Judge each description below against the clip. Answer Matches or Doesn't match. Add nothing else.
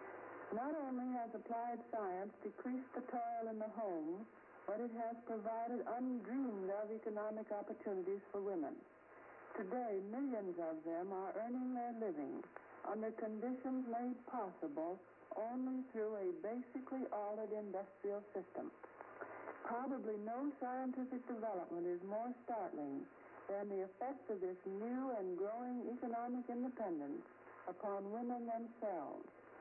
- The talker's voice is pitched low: Doesn't match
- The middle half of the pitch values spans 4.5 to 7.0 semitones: Doesn't match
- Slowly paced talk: Matches